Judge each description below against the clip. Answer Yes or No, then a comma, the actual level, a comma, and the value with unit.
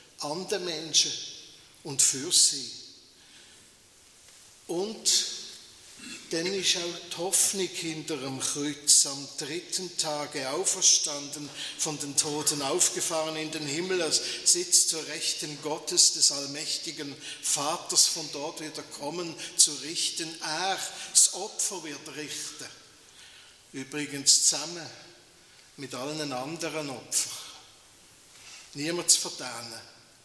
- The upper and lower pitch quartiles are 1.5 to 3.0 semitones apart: Yes, average, 2.7 semitones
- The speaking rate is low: Yes, slow, 105 wpm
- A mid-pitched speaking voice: Yes, medium, 155 Hz